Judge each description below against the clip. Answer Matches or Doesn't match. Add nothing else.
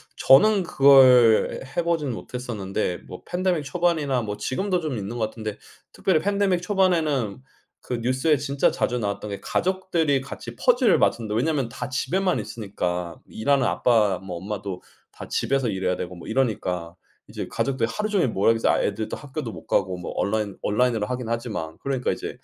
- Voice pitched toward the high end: Doesn't match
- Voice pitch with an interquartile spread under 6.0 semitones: Doesn't match